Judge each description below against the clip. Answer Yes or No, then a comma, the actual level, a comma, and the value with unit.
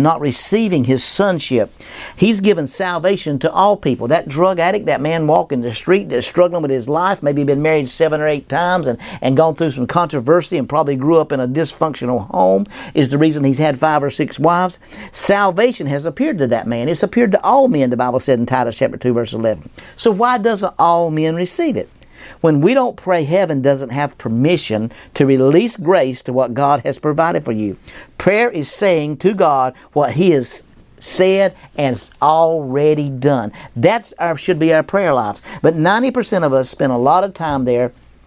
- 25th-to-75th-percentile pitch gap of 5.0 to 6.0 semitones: Yes, average, 5.3 semitones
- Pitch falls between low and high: Yes, medium, 155 Hz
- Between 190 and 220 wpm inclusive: Yes, average, 200 wpm